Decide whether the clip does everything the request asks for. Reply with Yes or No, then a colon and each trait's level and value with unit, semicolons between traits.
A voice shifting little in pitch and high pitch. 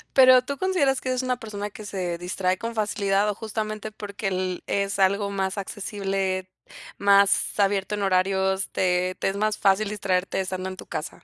Yes: narrow, 1.9 semitones; high, 200 Hz